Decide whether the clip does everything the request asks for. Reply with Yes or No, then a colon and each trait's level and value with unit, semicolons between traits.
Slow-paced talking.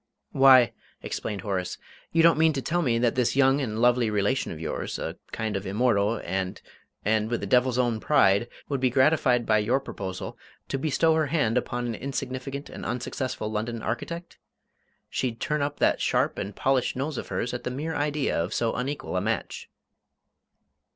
No: average, 185 wpm